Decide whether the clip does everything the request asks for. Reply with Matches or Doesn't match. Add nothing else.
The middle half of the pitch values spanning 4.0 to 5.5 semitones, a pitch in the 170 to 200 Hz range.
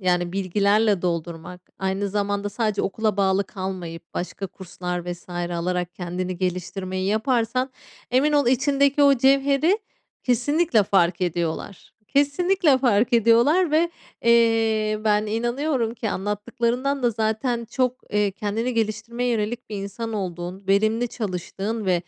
Doesn't match